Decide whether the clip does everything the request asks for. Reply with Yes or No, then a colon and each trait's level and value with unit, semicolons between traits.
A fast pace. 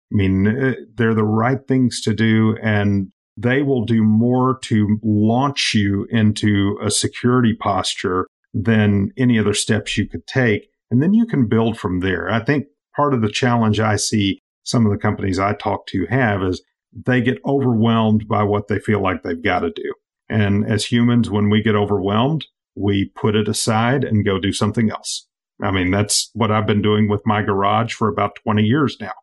No: average, 195 wpm